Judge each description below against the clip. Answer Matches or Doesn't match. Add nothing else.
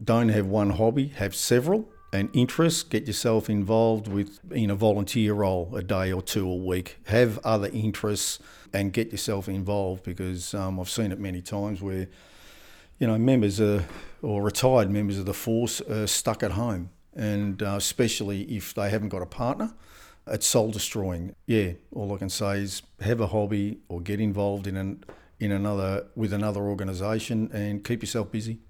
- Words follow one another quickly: Doesn't match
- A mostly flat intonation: Matches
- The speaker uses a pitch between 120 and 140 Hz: Doesn't match